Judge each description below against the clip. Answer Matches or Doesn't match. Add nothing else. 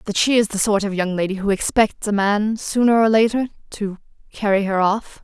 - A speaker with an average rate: Doesn't match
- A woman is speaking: Matches